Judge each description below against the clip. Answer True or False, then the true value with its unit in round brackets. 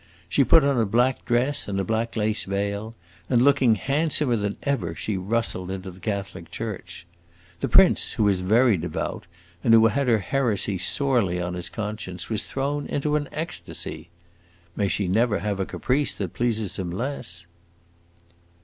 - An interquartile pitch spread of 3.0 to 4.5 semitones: False (5.0 semitones)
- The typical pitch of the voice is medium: False (110 Hz)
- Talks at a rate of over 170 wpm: False (165 wpm)